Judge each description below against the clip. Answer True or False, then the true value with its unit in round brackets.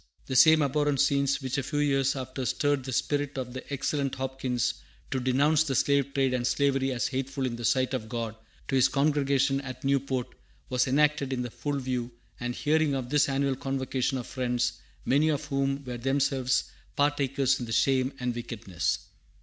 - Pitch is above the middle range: False (135 Hz)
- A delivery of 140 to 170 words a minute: False (185 wpm)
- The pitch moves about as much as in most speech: False (1.7 semitones)